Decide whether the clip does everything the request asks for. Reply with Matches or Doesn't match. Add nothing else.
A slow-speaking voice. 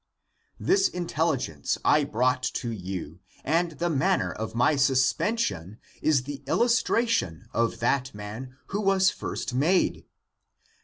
Matches